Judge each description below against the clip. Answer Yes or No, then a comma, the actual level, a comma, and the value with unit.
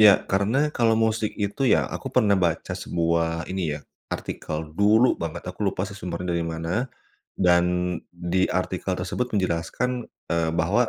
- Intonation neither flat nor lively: Yes, average, 3.9 semitones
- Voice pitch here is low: Yes, very low, 95 Hz